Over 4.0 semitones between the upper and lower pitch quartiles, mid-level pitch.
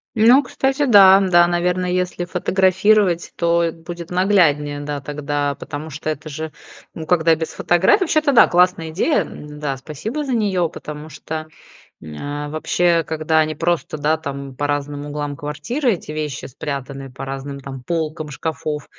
No: average, 3.6 semitones; medium, 160 Hz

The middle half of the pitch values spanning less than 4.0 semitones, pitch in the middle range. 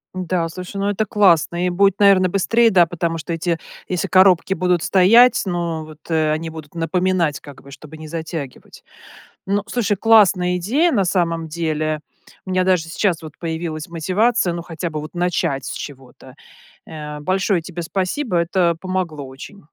Yes: average, 2.9 semitones; medium, 175 Hz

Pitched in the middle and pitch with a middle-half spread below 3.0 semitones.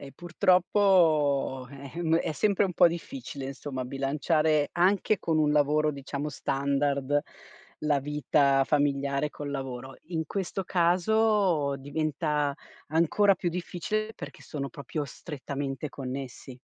No: medium, 150 Hz; average, 3.8 semitones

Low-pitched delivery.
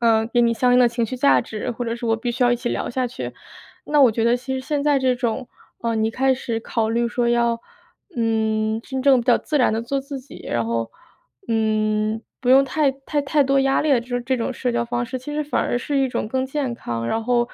No: high, 245 Hz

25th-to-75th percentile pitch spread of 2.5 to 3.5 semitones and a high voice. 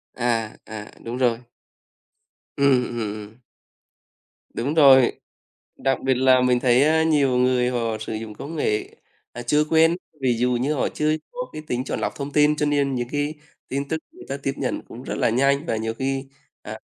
No: average, 3.2 semitones; low, 130 Hz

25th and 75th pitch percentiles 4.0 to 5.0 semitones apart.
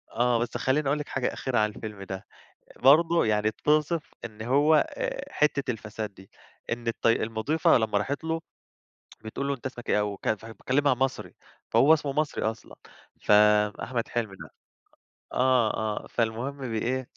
Yes: average, 4.5 semitones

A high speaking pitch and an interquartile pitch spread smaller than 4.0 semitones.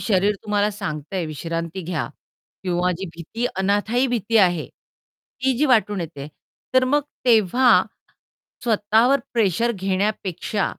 No: high, 205 Hz; average, 4.4 semitones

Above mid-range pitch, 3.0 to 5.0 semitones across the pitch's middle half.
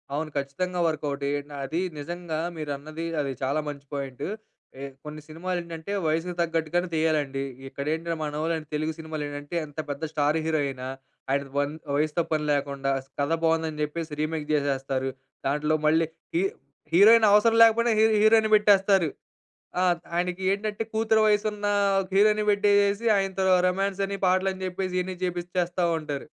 No: medium, 165 Hz; average, 4.4 semitones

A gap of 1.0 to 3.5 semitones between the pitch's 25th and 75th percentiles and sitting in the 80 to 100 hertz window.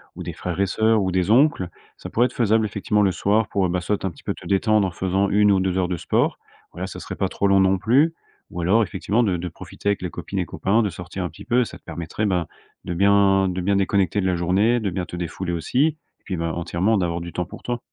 Yes: average, 2.9 semitones; very low, 95 Hz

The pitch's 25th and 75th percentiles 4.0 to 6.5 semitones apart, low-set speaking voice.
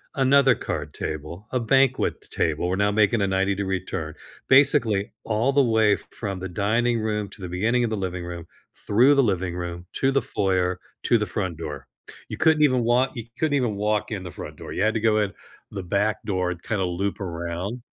Yes: average, 4.6 semitones; low, 100 Hz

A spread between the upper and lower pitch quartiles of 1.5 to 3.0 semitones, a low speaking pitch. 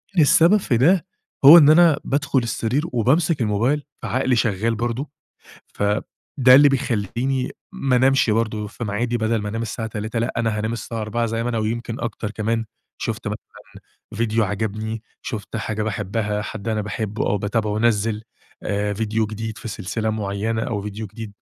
Yes: narrow, 2.4 semitones; low, 115 Hz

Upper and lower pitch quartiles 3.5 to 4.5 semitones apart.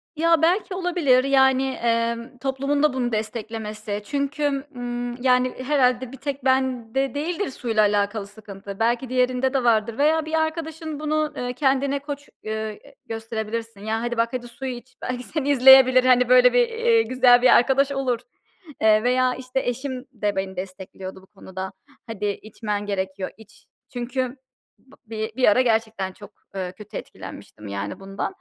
Yes: average, 3.8 semitones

